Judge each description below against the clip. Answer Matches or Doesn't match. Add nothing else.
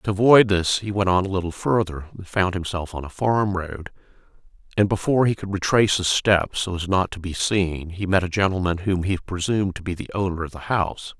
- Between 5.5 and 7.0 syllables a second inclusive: Matches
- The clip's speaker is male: Matches